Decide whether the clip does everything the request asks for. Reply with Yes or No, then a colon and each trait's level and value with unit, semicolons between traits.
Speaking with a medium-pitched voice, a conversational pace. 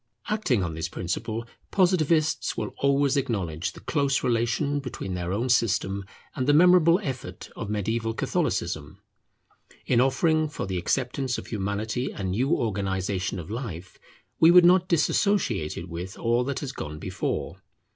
No: low, 120 Hz; average, 150 wpm